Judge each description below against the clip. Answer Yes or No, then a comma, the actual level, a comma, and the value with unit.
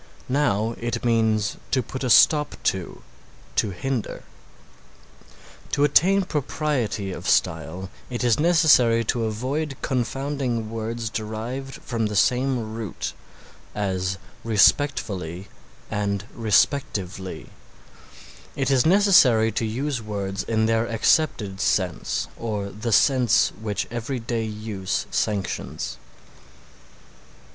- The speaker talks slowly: Yes, slow, 105 wpm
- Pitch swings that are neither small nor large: Yes, average, 4.0 semitones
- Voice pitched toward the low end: Yes, low, 115 Hz